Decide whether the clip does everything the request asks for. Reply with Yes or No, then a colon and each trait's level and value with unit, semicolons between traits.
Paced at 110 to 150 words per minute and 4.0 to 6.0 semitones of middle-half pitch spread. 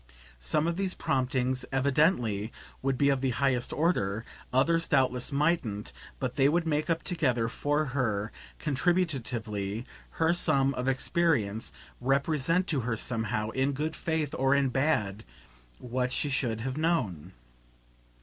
Yes: average, 140 wpm; average, 4.7 semitones